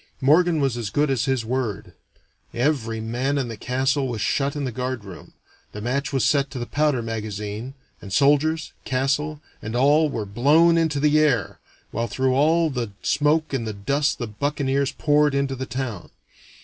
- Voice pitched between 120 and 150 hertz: Yes, low, 135 Hz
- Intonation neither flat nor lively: Yes, average, 4.1 semitones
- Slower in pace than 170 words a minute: No, average, 180 wpm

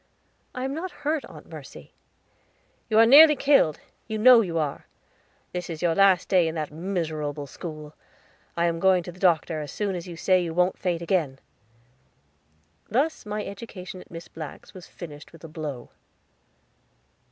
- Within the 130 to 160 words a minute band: No, average, 170 wpm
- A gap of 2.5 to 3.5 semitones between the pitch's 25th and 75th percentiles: No, average, 4.4 semitones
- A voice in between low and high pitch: Yes, medium, 175 Hz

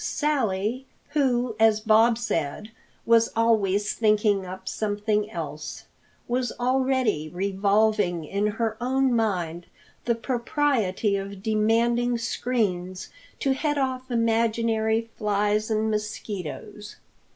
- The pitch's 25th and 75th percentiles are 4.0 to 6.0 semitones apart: No, average, 2.9 semitones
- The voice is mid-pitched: No, high, 220 Hz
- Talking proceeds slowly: Yes, slow, 105 wpm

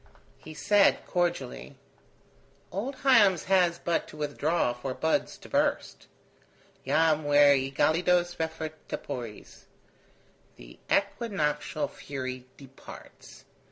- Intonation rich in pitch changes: No, average, 4.2 semitones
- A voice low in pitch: No, medium, 155 Hz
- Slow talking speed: Yes, slow, 95 wpm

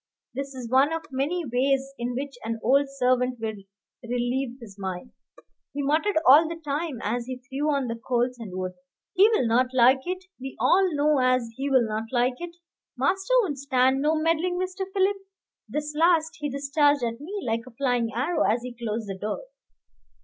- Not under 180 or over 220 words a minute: Yes, average, 185 wpm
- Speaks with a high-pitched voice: Yes, very high, 265 Hz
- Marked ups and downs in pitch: No, average, 4.1 semitones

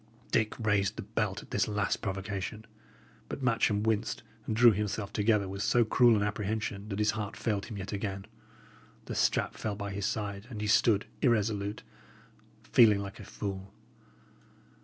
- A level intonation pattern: Yes, narrow, 1.7 semitones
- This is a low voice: Yes, low, 105 Hz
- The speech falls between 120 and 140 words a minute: No, average, 165 wpm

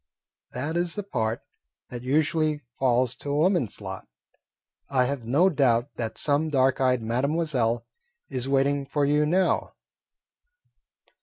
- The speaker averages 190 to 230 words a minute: No, slow, 135 wpm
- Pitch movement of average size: Yes, average, 3.5 semitones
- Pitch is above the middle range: No, low, 135 Hz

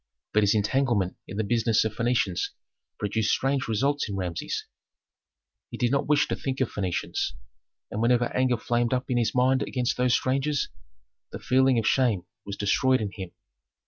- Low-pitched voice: Yes, low, 120 Hz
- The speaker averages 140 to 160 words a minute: No, average, 175 wpm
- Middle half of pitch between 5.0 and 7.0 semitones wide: No, average, 3.9 semitones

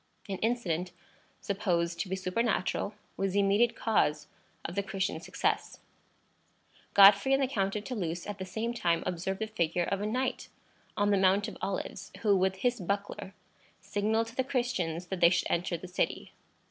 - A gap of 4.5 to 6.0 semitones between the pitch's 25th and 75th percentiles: No, average, 3.1 semitones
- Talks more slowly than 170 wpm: No, average, 175 wpm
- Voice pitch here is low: No, high, 195 Hz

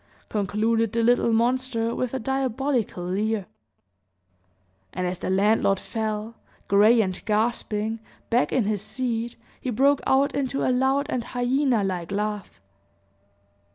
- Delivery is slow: Yes, slow, 130 wpm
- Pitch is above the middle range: Yes, high, 225 Hz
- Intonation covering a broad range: No, average, 3.4 semitones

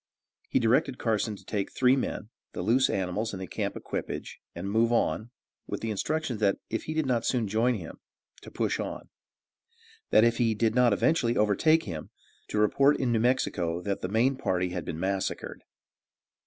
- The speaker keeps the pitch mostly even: No, average, 4.1 semitones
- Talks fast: No, average, 185 wpm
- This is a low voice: Yes, low, 110 Hz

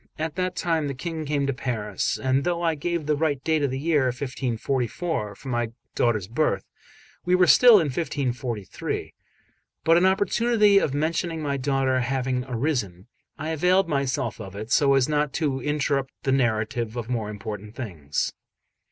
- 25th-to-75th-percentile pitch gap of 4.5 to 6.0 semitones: Yes, average, 5.0 semitones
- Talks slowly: No, average, 170 wpm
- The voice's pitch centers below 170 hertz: Yes, medium, 140 Hz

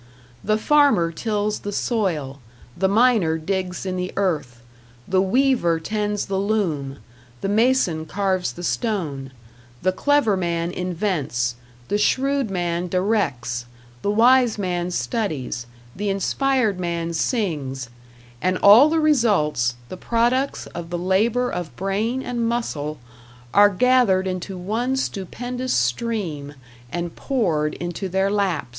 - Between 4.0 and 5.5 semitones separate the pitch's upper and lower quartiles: Yes, average, 5.1 semitones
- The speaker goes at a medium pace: No, slow, 125 wpm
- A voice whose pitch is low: No, high, 190 Hz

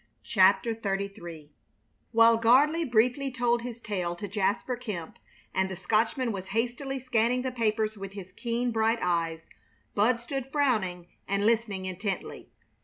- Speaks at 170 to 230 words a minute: No, average, 140 wpm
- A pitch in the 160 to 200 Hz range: No, high, 225 Hz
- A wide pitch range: No, average, 3.9 semitones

